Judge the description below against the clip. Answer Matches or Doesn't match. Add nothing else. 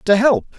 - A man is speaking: Matches